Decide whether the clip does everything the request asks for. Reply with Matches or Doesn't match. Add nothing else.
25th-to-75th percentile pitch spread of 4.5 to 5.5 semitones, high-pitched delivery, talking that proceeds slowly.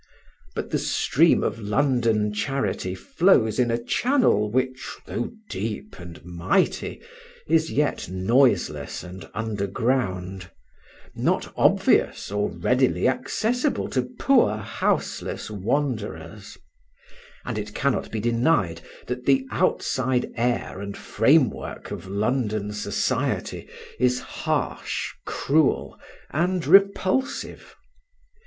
Doesn't match